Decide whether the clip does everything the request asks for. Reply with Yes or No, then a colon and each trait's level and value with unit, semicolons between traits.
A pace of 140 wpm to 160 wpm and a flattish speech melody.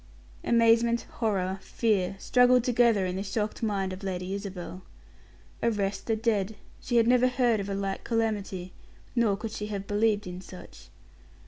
No: average, 155 wpm; average, 3.1 semitones